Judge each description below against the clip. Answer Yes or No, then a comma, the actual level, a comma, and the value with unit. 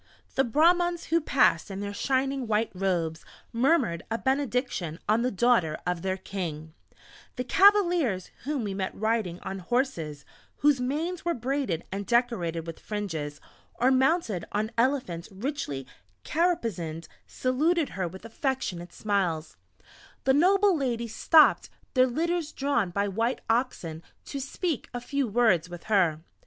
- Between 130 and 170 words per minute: Yes, average, 140 wpm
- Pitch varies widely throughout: Yes, wide, 7.2 semitones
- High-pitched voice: Yes, high, 230 Hz